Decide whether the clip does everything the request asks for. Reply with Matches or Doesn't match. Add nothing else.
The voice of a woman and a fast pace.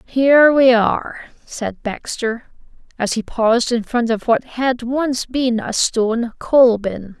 Doesn't match